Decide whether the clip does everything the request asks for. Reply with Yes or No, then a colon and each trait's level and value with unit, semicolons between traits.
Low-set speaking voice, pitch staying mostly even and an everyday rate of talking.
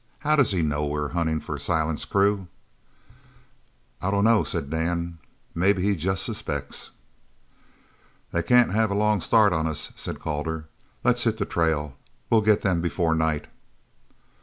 No: very low, 85 Hz; average, 4.3 semitones; average, 155 wpm